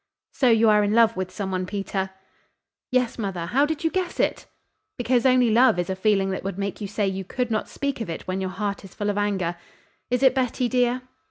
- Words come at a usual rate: No, fast, 235 wpm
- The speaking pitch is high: Yes, high, 210 Hz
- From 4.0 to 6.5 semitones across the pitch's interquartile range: Yes, average, 4.5 semitones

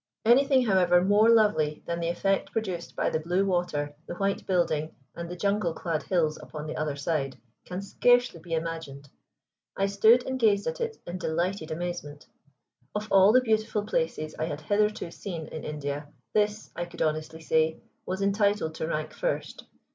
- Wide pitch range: No, average, 4.6 semitones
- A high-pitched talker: No, medium, 175 Hz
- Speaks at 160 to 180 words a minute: Yes, average, 175 wpm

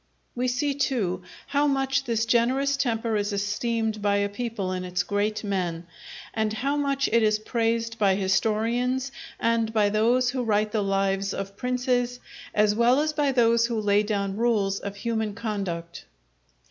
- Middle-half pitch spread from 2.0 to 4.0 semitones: Yes, average, 3.5 semitones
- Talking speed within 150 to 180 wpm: Yes, average, 165 wpm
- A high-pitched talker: Yes, high, 225 Hz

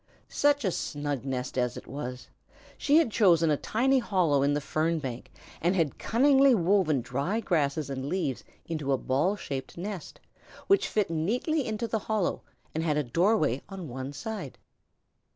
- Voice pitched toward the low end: No, medium, 165 Hz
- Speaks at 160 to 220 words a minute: Yes, average, 170 wpm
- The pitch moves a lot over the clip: Yes, wide, 7.2 semitones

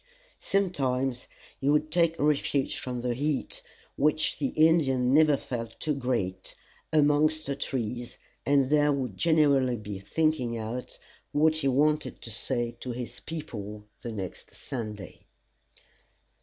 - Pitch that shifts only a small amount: No, average, 4.1 semitones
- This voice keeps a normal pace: No, slow, 130 wpm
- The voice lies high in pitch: No, low, 135 Hz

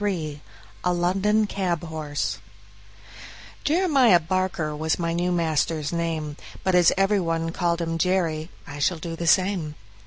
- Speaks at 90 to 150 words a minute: Yes, average, 145 wpm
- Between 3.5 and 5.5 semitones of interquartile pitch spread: No, average, 2.7 semitones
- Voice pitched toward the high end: No, medium, 170 Hz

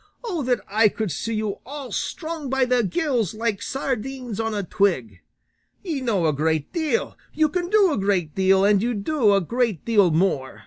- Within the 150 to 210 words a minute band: Yes, average, 190 wpm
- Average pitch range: No, wide, 5.7 semitones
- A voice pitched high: Yes, high, 225 Hz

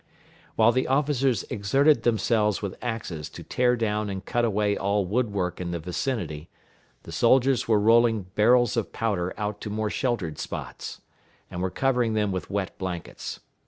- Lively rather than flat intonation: No, average, 3.7 semitones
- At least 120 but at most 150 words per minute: No, average, 170 wpm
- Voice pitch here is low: Yes, low, 105 Hz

